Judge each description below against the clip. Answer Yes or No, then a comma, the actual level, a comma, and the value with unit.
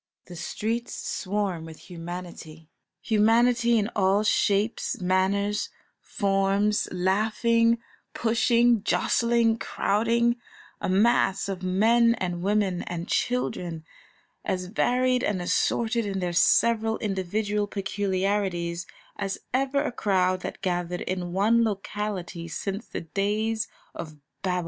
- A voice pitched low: No, high, 200 Hz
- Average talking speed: No, slow, 110 wpm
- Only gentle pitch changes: No, average, 3.7 semitones